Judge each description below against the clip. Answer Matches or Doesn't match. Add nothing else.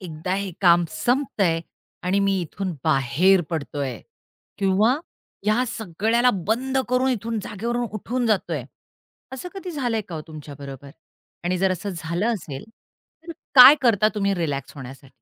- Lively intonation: Matches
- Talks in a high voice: Matches